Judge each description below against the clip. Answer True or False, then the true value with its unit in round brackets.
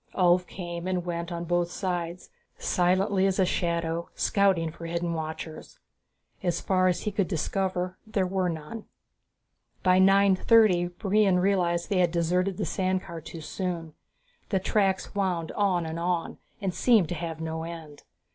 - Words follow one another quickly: False (160 wpm)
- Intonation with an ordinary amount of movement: False (2.1 semitones)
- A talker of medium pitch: True (180 Hz)